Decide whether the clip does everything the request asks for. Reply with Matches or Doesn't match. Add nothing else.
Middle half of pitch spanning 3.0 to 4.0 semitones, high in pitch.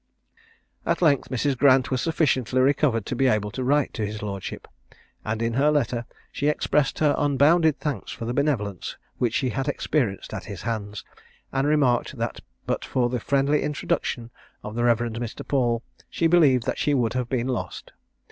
Doesn't match